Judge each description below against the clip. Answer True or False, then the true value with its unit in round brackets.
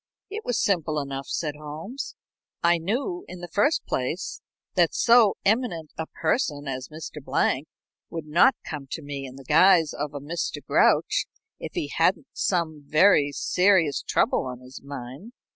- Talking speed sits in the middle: True (160 wpm)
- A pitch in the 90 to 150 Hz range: False (160 Hz)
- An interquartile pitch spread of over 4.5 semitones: True (5.1 semitones)